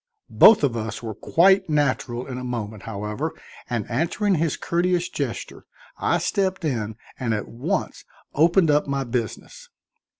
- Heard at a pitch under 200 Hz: Yes, medium, 140 Hz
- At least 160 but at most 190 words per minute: No, average, 145 wpm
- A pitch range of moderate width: No, wide, 6.9 semitones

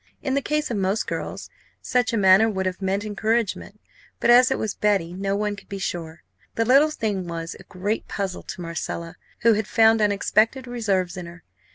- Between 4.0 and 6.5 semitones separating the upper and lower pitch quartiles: No, average, 3.4 semitones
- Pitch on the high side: Yes, high, 205 Hz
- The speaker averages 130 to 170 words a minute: No, average, 200 wpm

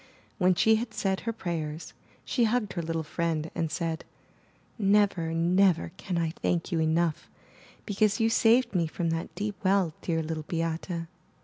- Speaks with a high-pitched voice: No, medium, 170 Hz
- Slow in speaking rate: No, average, 165 wpm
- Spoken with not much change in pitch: No, average, 3.8 semitones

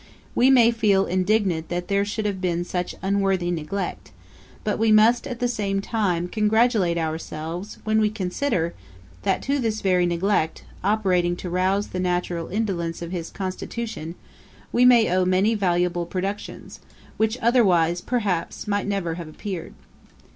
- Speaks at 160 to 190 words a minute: No, average, 145 wpm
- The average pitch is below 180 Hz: No, high, 195 Hz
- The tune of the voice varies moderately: Yes, average, 3.6 semitones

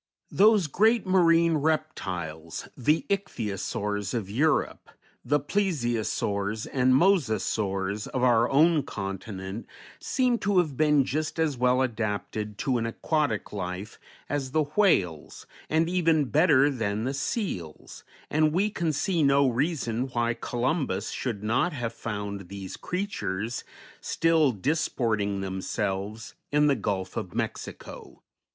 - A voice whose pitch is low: Yes, low, 125 Hz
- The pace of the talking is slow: Yes, slow, 125 wpm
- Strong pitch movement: Yes, wide, 7.2 semitones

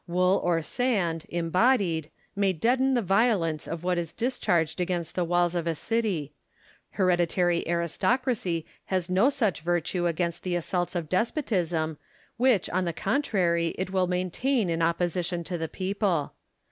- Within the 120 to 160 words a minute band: Yes, average, 145 wpm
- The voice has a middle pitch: Yes, medium, 180 Hz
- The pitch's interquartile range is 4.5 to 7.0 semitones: No, average, 2.8 semitones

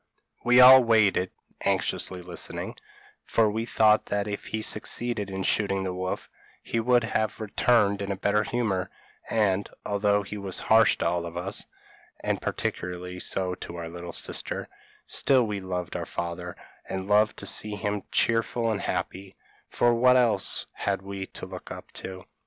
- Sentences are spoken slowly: No, average, 165 wpm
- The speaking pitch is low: Yes, low, 100 Hz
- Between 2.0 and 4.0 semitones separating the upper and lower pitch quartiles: Yes, average, 3.1 semitones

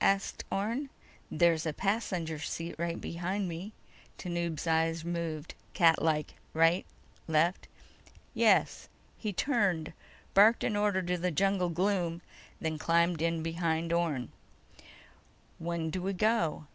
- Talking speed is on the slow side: Yes, slow, 120 wpm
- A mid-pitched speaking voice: Yes, medium, 170 Hz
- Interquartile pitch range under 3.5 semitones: Yes, average, 2.7 semitones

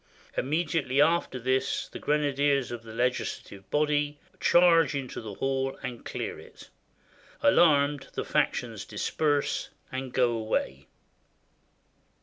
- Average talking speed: No, slow, 125 wpm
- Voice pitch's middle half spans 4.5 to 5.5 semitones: No, average, 2.9 semitones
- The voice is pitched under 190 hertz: Yes, low, 135 Hz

